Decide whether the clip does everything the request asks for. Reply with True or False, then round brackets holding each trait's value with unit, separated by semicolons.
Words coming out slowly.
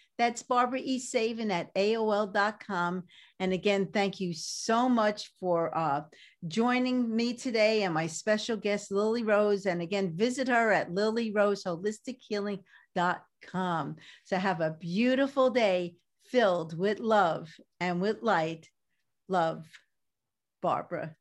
True (120 wpm)